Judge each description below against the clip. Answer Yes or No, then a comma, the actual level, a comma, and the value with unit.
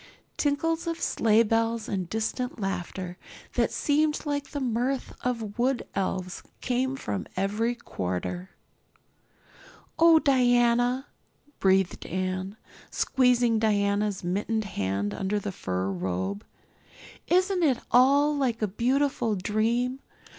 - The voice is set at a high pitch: Yes, high, 225 Hz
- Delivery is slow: Yes, slow, 110 wpm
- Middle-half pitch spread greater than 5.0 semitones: Yes, wide, 5.6 semitones